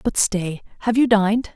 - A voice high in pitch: Yes, high, 210 Hz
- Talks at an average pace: Yes, average, 155 wpm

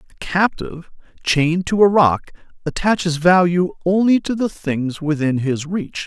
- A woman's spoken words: No, male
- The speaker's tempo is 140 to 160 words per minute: Yes, average, 150 wpm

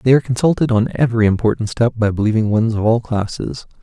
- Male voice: Yes, male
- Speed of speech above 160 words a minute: Yes, fast, 205 wpm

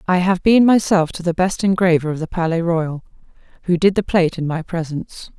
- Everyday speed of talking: No, fast, 210 wpm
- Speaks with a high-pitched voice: No, medium, 175 Hz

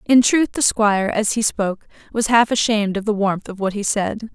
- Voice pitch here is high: Yes, high, 215 Hz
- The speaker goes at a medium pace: No, fast, 235 wpm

